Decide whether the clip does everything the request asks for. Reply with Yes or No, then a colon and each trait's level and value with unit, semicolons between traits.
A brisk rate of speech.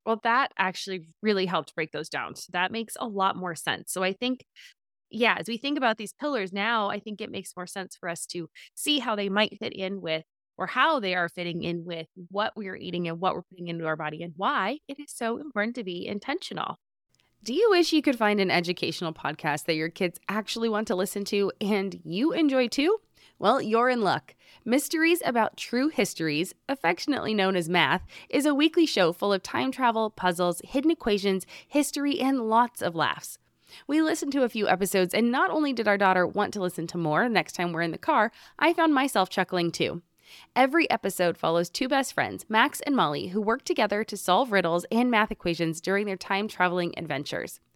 Yes: fast, 210 wpm